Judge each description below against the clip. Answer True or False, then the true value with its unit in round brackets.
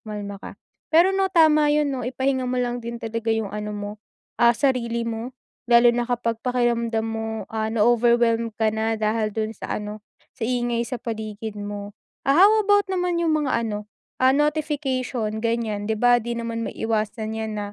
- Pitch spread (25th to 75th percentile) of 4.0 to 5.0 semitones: False (2.8 semitones)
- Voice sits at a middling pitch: False (235 Hz)